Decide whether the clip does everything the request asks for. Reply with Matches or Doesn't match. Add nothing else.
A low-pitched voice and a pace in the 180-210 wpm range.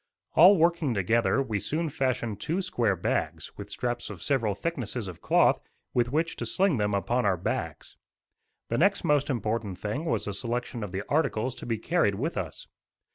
Matches